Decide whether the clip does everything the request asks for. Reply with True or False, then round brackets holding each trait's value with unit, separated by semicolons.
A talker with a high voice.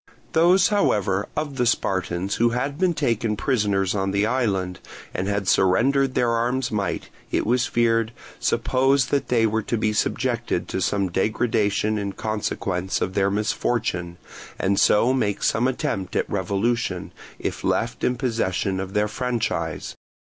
False (110 Hz)